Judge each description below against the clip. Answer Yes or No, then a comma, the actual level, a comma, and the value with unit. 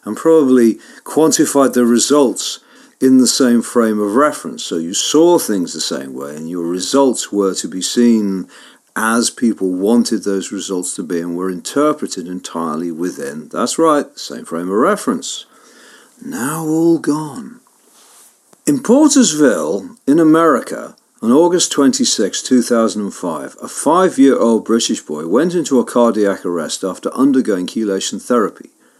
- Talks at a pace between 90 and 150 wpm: Yes, average, 140 wpm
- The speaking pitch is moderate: No, low, 120 Hz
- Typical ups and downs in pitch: No, wide, 7.5 semitones